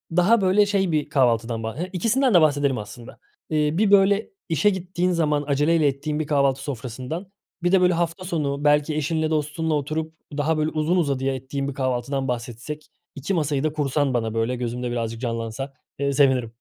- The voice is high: No, medium, 150 Hz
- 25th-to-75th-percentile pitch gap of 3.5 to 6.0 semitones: Yes, average, 4.0 semitones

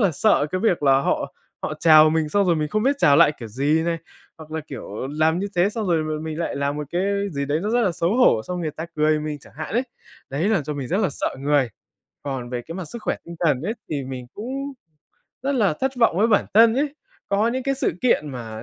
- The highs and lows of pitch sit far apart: Yes, wide, 6.3 semitones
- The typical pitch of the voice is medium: Yes, medium, 160 Hz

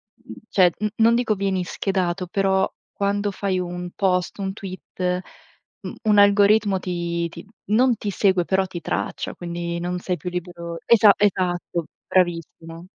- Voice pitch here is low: No, medium, 185 Hz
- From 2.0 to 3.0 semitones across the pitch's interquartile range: Yes, narrow, 2.3 semitones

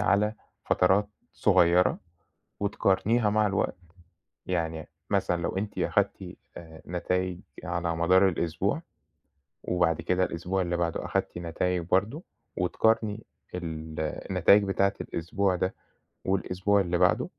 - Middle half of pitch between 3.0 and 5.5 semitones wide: No, narrow, 2.5 semitones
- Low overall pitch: Yes, very low, 90 Hz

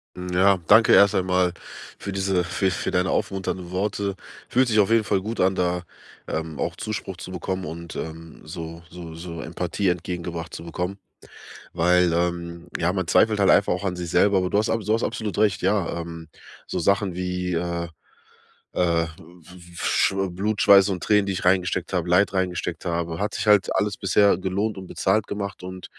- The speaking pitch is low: Yes, very low, 90 Hz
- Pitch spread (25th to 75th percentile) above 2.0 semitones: Yes, narrow, 2.5 semitones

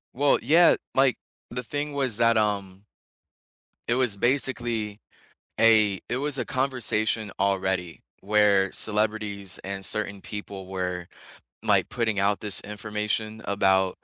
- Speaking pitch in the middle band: No, low, 105 Hz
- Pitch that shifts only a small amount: No, average, 3.3 semitones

